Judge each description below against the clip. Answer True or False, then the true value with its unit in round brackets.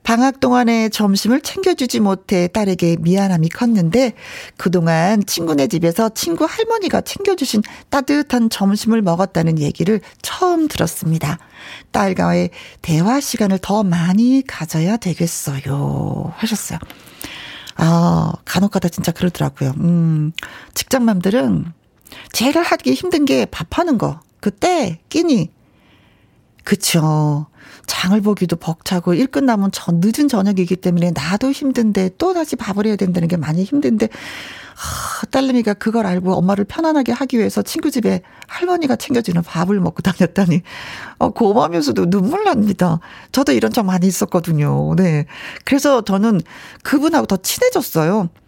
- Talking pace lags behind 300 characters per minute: False (305 characters per minute)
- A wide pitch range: True (6.6 semitones)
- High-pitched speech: True (200 Hz)